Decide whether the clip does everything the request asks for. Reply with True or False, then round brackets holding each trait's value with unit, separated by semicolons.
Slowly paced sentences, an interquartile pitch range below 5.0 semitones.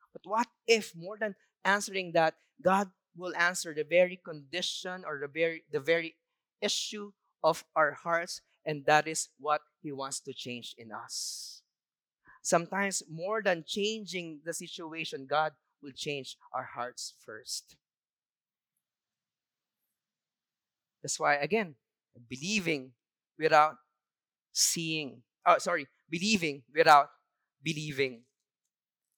True (115 wpm; 4.0 semitones)